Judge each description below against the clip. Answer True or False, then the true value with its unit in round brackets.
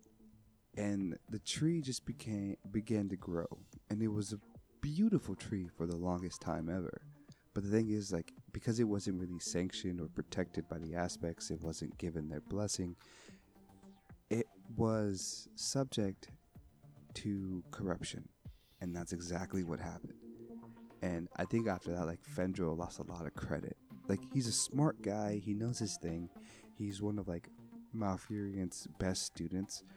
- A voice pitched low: True (100 Hz)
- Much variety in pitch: False (3.9 semitones)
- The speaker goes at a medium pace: True (155 wpm)